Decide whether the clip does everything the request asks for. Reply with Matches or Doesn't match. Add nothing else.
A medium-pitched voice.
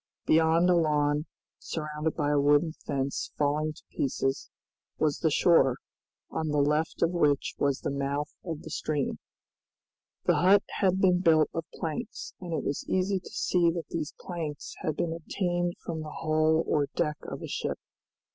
Matches